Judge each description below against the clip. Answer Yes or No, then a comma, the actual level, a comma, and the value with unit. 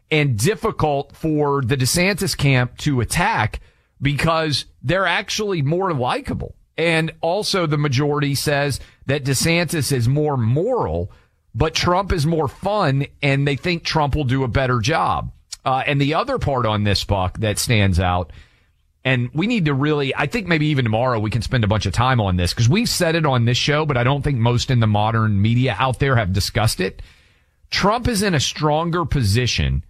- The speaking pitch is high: No, low, 135 Hz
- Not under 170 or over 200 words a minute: Yes, average, 185 wpm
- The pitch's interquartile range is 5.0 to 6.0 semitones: Yes, average, 5.3 semitones